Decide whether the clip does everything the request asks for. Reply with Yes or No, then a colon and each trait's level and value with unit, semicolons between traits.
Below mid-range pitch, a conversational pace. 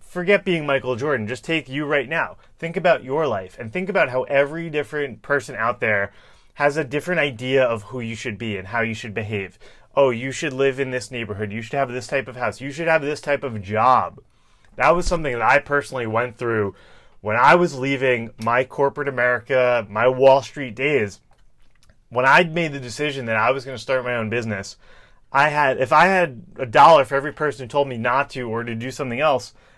No: low, 130 Hz; fast, 220 wpm